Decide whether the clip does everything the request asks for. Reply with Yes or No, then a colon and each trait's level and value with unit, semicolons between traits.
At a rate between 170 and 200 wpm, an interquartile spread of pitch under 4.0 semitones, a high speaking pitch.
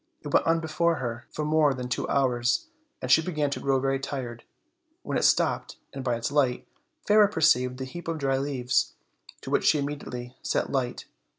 No: average, 195 wpm; average, 3.5 semitones; low, 135 Hz